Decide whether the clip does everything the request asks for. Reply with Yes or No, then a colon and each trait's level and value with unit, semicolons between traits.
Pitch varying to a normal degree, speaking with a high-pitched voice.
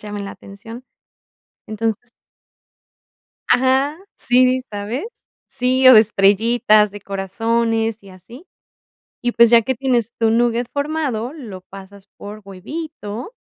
Yes: average, 3.6 semitones; high, 230 Hz